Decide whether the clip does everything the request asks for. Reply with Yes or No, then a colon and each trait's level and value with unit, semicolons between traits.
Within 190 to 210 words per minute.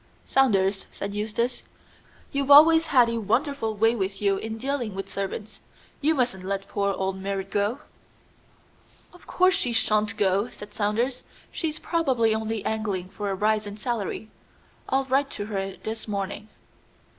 No: average, 155 wpm